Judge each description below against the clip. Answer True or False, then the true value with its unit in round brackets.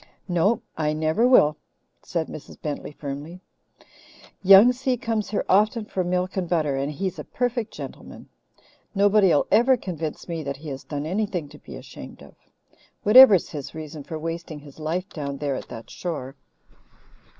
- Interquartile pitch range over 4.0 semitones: True (5.3 semitones)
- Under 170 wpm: True (160 wpm)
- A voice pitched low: False (170 Hz)